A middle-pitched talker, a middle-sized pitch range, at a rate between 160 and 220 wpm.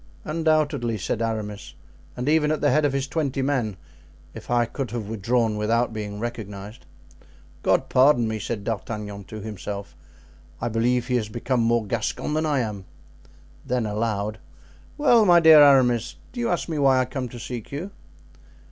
No: low, 120 Hz; average, 4.6 semitones; average, 170 wpm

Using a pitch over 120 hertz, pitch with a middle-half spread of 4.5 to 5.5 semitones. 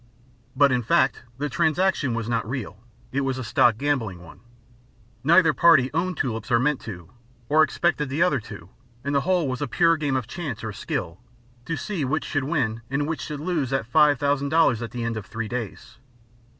Yes: low, 135 Hz; average, 4.9 semitones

